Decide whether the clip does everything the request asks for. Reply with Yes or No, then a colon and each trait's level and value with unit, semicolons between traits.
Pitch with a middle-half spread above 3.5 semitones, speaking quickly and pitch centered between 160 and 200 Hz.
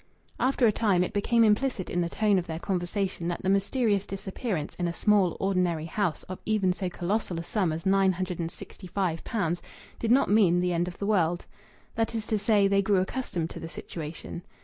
No: average, 3.2 semitones; fast, 215 wpm; high, 190 Hz